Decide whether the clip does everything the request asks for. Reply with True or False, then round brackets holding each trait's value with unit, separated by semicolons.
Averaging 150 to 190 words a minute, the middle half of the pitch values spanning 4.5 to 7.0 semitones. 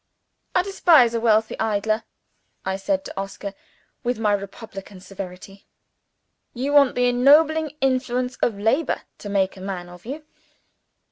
False (140 wpm; 5.2 semitones)